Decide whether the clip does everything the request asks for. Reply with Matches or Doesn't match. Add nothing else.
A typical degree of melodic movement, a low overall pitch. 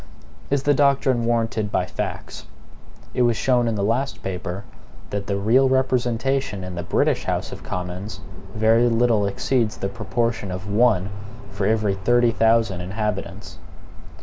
Matches